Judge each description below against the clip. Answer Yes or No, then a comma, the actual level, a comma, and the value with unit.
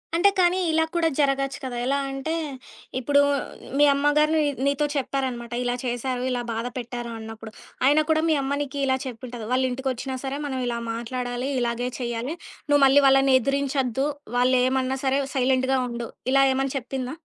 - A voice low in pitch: No, very high, 265 Hz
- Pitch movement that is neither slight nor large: No, narrow, 2.1 semitones